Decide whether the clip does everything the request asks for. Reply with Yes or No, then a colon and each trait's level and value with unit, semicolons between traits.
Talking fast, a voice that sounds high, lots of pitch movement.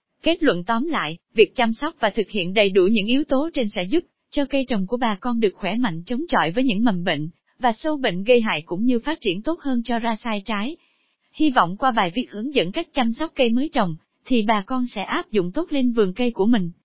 No: fast, 260 wpm; high, 240 Hz; average, 4.6 semitones